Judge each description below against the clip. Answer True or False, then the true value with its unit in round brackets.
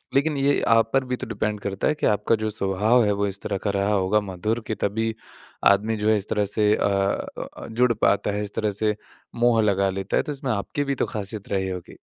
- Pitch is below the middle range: True (105 Hz)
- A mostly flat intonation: True (2.2 semitones)